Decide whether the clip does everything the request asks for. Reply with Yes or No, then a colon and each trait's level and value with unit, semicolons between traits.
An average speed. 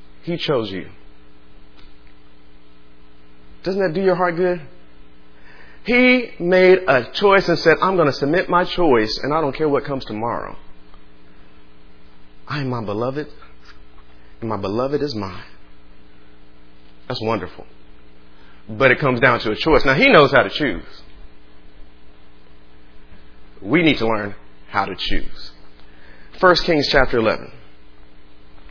No: slow, 130 wpm